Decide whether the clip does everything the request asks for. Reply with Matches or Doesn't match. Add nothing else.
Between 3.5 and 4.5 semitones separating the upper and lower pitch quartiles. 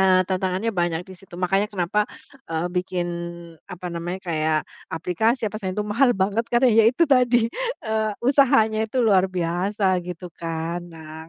Matches